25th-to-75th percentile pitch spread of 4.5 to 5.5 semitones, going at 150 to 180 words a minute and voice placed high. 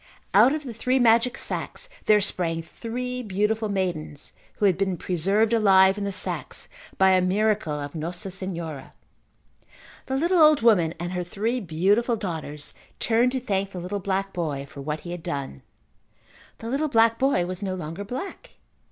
Yes: average, 4.8 semitones; average, 170 wpm; high, 195 Hz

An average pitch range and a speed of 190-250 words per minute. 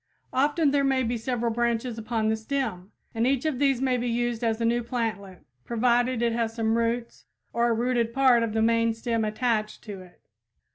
No: narrow, 1.8 semitones; average, 200 wpm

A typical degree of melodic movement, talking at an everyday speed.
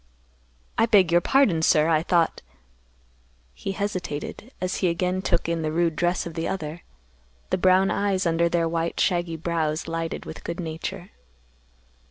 No: narrow, 2.1 semitones; average, 160 wpm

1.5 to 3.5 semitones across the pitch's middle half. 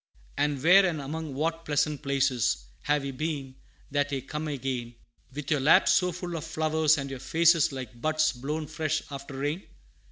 Yes: narrow, 2.6 semitones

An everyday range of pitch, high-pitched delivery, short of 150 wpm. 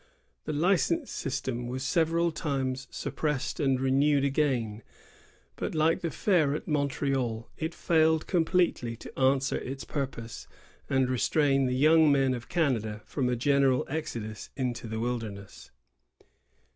No: average, 3.8 semitones; low, 135 Hz; slow, 135 wpm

